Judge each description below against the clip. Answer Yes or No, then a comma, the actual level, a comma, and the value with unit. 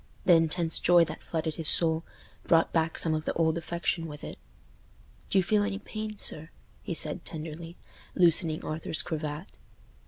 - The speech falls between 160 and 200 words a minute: Yes, average, 165 wpm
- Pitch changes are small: Yes, narrow, 1.7 semitones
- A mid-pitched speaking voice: Yes, medium, 165 Hz